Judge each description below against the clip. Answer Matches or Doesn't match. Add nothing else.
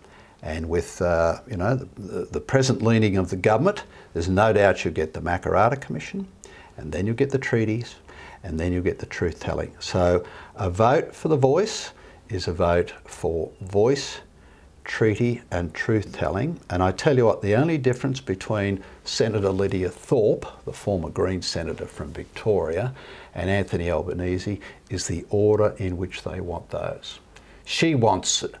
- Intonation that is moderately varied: Matches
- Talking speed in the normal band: Matches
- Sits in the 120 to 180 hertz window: Doesn't match